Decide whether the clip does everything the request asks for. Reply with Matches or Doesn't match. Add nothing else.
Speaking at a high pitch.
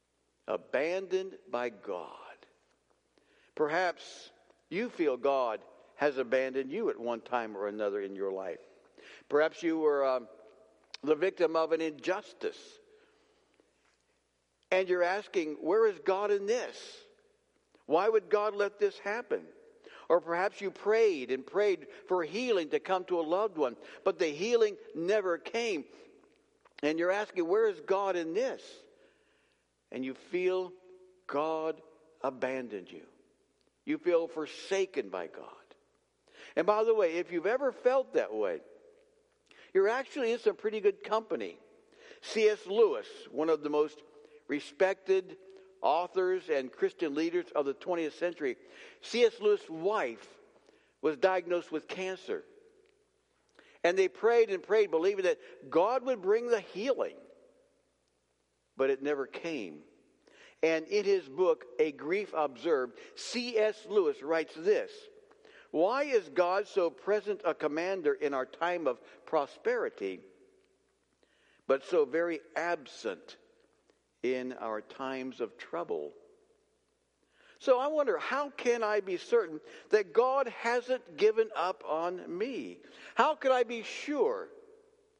Matches